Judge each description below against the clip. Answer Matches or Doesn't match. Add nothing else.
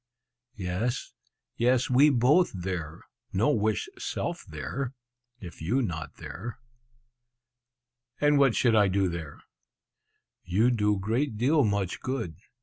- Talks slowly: Matches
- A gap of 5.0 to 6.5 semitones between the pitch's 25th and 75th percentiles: Matches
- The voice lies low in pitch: Matches